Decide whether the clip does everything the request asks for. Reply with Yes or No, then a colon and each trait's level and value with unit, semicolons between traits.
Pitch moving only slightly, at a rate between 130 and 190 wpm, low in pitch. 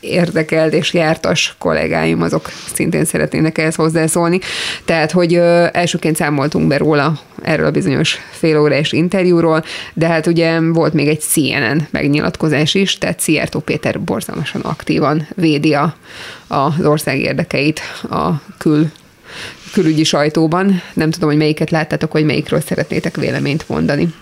No: narrow, 1.8 semitones; average, 135 wpm; medium, 160 Hz